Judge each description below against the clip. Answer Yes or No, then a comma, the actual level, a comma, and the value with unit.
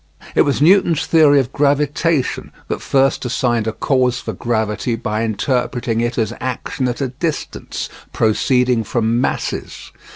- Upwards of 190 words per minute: No, average, 140 wpm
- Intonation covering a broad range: No, average, 3.5 semitones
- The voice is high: No, low, 125 Hz